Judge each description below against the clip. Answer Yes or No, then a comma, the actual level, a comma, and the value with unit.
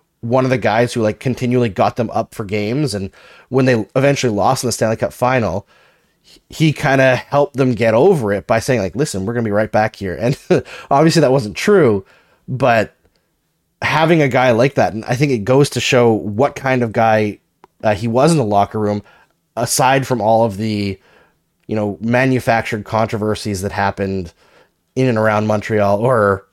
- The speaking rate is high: No, average, 190 wpm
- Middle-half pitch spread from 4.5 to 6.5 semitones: No, average, 3.7 semitones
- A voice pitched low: Yes, low, 115 Hz